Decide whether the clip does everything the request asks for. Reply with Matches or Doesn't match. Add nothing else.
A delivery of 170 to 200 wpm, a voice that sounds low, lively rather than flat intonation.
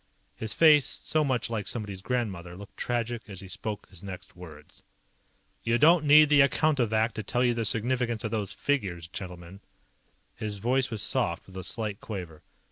Doesn't match